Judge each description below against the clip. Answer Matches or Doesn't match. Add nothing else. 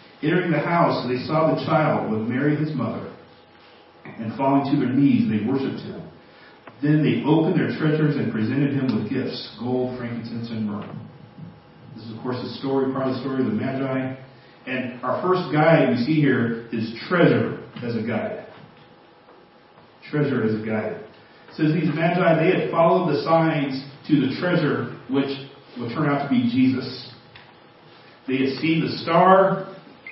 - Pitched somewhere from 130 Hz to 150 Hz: Matches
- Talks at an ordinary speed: Matches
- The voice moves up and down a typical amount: Matches